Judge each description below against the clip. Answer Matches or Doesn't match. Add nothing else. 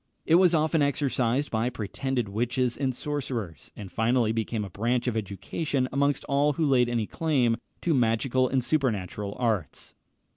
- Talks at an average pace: Matches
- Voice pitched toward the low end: Matches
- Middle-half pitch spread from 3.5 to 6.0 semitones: Matches